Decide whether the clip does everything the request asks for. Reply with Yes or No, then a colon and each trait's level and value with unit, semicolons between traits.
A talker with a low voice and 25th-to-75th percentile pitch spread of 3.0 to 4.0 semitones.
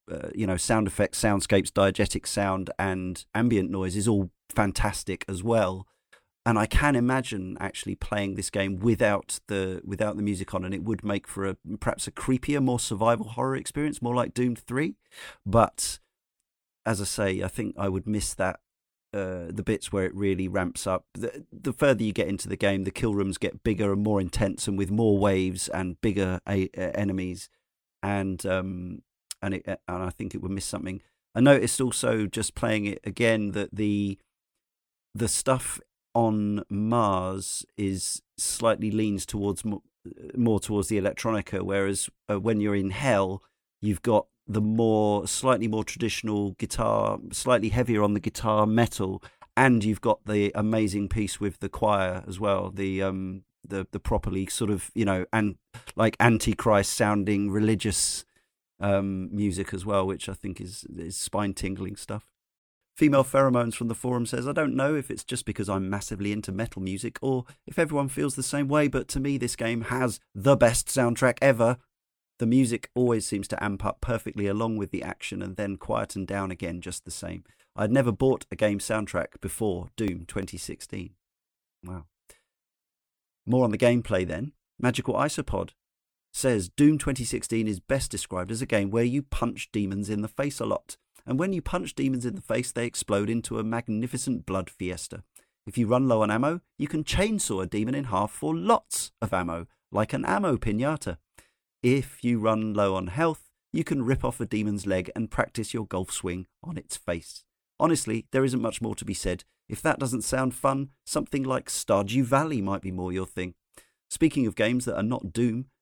Yes: low, 105 Hz; average, 3.6 semitones